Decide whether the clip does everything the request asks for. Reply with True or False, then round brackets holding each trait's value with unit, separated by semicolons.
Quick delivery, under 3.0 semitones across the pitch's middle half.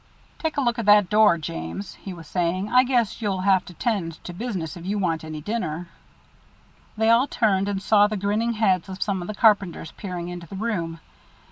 False (210 wpm; 4.0 semitones)